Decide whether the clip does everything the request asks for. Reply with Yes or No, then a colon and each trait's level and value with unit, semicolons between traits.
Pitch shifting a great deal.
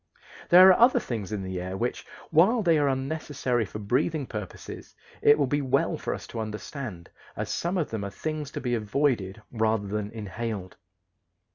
Yes: wide, 5.7 semitones